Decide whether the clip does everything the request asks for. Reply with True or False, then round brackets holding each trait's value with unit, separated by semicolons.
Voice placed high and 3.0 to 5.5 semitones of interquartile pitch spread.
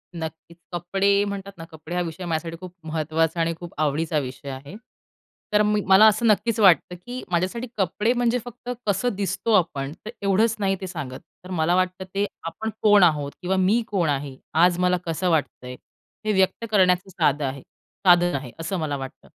False (180 Hz; 3.9 semitones)